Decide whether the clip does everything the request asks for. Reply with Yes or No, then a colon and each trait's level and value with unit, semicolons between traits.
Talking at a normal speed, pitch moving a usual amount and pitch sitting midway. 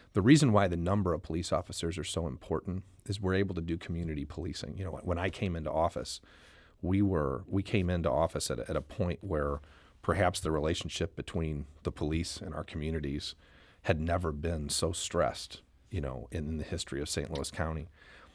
No: average, 195 wpm; average, 3.3 semitones; very low, 85 Hz